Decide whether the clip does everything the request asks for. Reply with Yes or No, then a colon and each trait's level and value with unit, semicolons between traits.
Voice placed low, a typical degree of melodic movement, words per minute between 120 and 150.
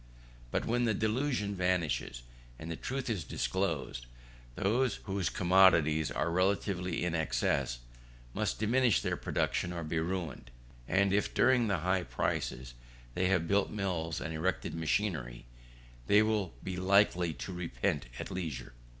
Yes: very low, 90 Hz; average, 3.9 semitones; average, 140 wpm